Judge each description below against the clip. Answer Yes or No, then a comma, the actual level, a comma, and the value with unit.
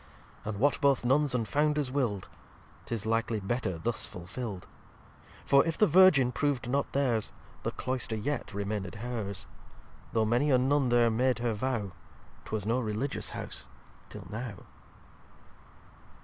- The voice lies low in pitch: Yes, low, 120 Hz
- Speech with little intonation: No, average, 4.1 semitones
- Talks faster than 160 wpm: No, average, 140 wpm